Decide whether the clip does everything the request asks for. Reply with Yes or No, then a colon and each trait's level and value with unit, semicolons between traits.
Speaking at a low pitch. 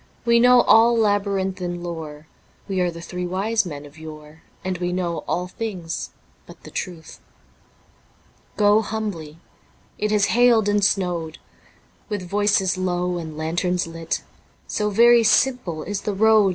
No: medium, 185 Hz